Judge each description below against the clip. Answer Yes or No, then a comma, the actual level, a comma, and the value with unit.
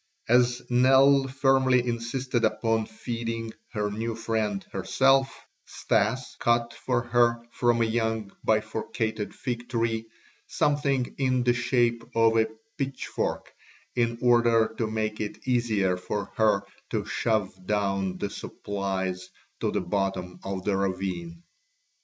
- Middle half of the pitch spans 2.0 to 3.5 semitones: Yes, average, 2.8 semitones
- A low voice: Yes, low, 115 Hz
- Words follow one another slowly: Yes, slow, 125 wpm